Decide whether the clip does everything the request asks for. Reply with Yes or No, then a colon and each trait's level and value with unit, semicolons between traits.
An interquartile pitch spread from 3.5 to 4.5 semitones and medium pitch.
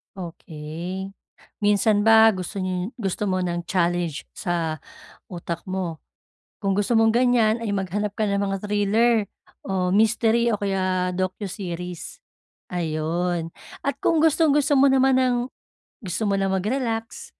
No: average, 3.8 semitones; high, 195 Hz